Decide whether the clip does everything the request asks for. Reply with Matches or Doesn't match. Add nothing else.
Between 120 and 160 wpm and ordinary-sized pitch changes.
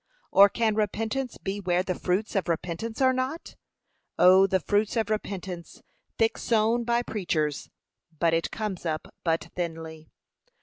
Matches